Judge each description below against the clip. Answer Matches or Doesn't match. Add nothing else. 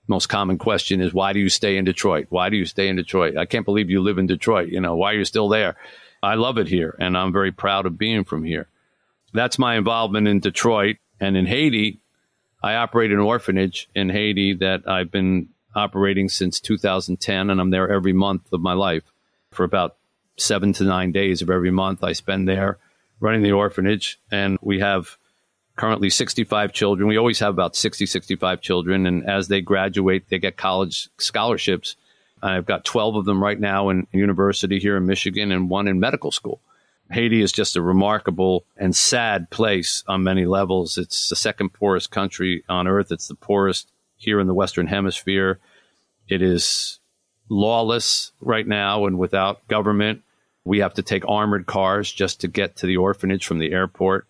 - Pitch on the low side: Matches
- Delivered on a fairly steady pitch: Matches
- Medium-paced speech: Matches